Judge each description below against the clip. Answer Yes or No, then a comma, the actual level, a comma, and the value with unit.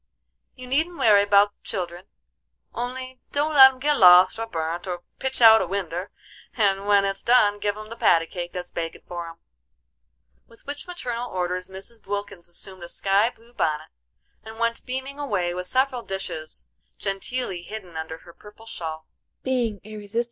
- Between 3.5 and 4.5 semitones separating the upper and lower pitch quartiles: No, average, 5.3 semitones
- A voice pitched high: Yes, high, 200 Hz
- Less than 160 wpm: No, average, 165 wpm